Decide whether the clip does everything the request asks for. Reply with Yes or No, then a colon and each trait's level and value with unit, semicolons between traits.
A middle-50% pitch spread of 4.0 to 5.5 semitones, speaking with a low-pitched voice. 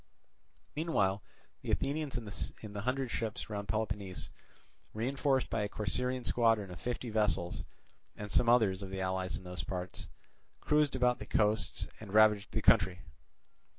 Yes: average, 4.3 semitones; low, 105 Hz